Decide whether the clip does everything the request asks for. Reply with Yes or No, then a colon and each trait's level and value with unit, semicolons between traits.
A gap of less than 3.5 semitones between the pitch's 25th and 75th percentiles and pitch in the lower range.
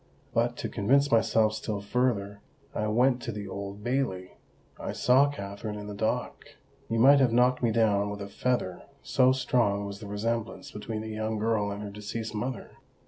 Yes: average, 3.1 semitones; low, 110 Hz